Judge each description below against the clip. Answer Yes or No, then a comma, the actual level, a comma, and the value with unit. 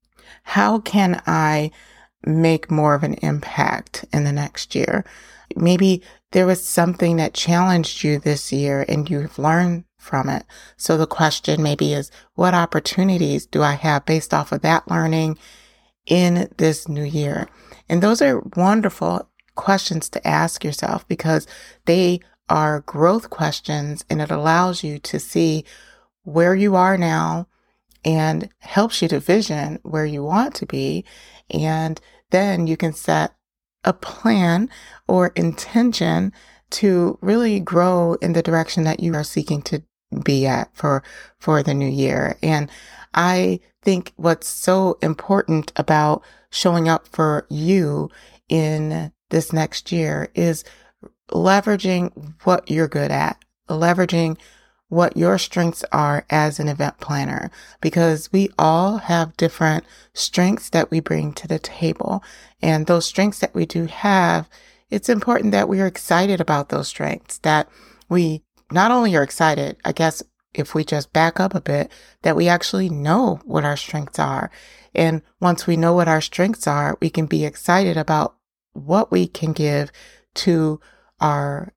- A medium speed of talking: Yes, average, 150 wpm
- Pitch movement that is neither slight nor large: Yes, average, 3.1 semitones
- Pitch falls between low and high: Yes, medium, 165 Hz